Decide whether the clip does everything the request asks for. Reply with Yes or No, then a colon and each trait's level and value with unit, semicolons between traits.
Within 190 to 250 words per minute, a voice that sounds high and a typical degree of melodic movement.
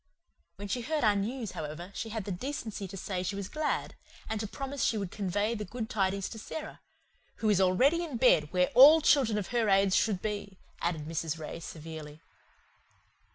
Yes: average, 195 wpm; high, 205 Hz; average, 4.3 semitones